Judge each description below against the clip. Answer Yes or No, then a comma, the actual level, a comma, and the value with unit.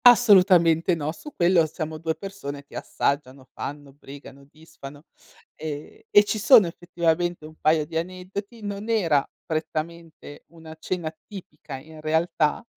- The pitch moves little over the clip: No, average, 3.3 semitones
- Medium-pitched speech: Yes, medium, 160 Hz